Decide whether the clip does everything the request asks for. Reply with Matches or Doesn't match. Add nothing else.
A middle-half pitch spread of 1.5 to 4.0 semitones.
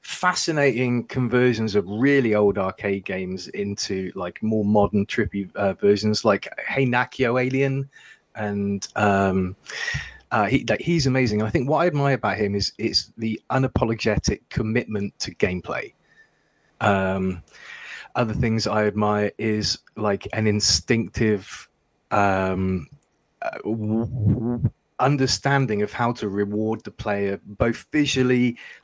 Matches